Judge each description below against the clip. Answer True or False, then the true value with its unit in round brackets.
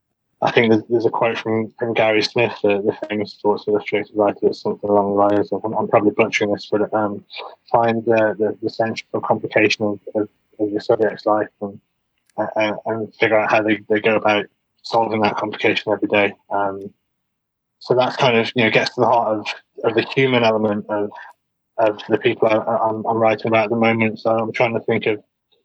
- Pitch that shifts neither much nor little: False (1.4 semitones)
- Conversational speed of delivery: False (210 wpm)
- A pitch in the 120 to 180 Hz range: False (110 Hz)